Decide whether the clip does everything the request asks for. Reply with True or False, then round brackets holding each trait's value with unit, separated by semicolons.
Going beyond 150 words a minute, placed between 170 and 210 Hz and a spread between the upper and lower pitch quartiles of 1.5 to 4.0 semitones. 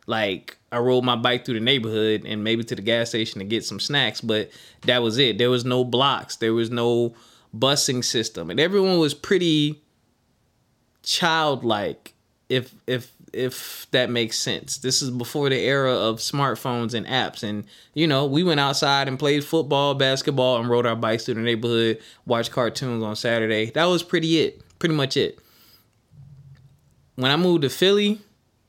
False (175 wpm; 125 Hz; 3.3 semitones)